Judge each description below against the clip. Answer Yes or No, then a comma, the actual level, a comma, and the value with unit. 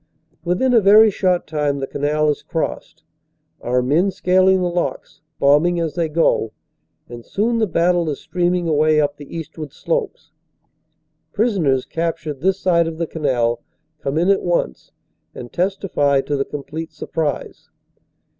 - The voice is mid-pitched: Yes, medium, 165 Hz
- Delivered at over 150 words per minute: Yes, average, 160 wpm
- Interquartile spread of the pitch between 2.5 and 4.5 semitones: Yes, average, 3.9 semitones